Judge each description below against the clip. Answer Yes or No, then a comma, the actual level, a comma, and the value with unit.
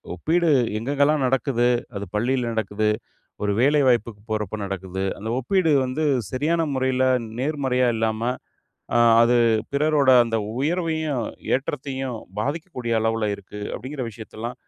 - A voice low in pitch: Yes, low, 130 Hz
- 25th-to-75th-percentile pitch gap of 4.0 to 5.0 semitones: Yes, average, 4.6 semitones